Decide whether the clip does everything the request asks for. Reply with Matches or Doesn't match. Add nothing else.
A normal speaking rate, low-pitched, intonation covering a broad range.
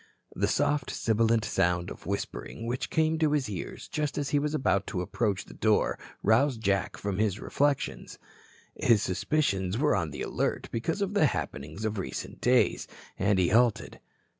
Matches